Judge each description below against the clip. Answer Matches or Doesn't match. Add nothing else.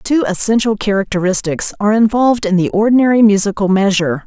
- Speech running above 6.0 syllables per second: Matches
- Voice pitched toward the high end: Matches